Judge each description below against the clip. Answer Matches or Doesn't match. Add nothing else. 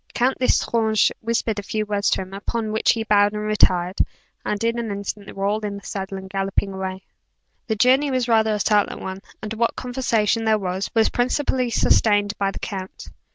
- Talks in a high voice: Matches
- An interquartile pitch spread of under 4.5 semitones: Matches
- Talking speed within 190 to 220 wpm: Matches